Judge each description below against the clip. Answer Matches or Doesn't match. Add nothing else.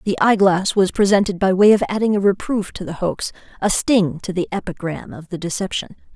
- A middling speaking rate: Matches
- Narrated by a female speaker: Matches